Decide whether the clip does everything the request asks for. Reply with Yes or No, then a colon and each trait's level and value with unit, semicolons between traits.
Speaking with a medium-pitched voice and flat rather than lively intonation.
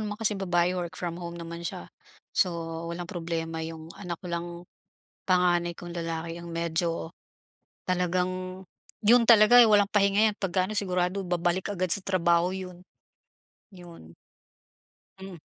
Yes: medium, 175 Hz; narrow, 1.9 semitones